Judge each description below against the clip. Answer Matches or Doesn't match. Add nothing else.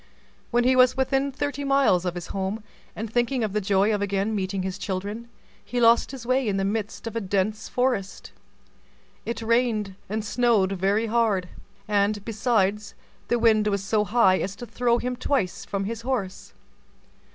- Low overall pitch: Doesn't match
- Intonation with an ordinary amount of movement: Matches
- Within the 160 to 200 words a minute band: Matches